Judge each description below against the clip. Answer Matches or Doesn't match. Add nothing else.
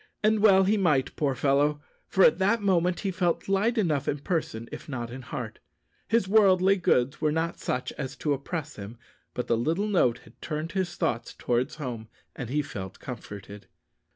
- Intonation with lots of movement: Matches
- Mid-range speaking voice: Matches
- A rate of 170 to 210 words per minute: Matches